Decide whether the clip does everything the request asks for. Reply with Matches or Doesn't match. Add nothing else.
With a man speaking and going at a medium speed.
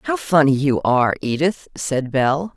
Doesn't match